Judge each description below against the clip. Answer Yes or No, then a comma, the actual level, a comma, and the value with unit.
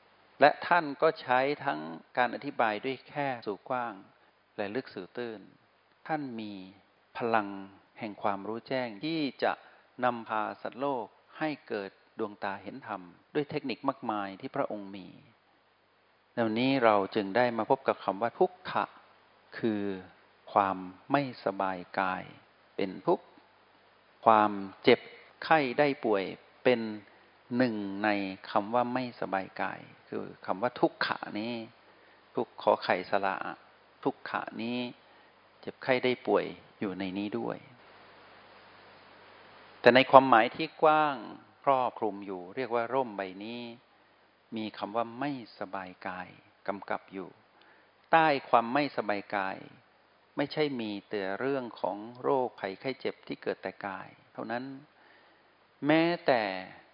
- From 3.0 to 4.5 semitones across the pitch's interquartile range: No, average, 5.0 semitones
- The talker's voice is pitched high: No, low, 115 Hz